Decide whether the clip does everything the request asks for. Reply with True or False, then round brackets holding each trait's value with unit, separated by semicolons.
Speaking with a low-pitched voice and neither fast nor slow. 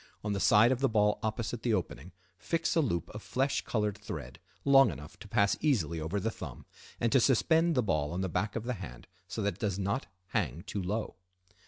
False (105 Hz; 220 wpm)